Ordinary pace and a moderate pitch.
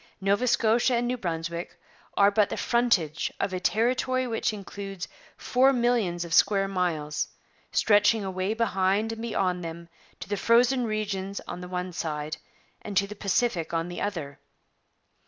No: average, 155 wpm; high, 200 Hz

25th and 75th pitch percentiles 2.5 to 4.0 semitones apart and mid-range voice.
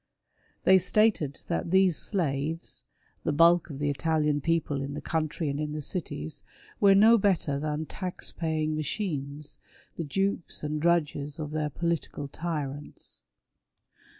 Yes: average, 2.9 semitones; medium, 155 Hz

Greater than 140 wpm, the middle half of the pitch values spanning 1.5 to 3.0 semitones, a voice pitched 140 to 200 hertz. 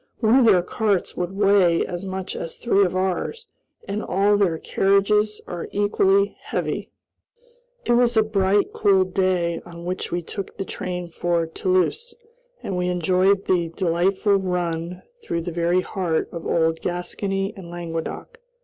Yes: average, 155 wpm; narrow, 2.5 semitones; medium, 185 Hz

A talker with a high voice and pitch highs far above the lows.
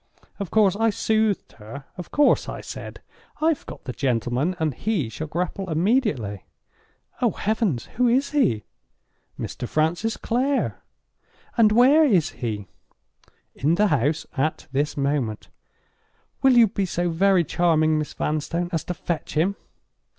No: medium, 175 Hz; wide, 7.3 semitones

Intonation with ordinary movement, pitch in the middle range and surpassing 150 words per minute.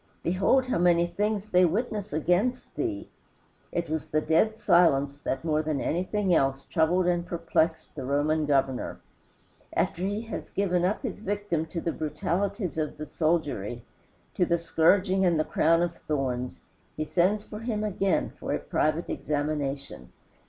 Yes: average, 4.3 semitones; medium, 170 Hz; average, 160 wpm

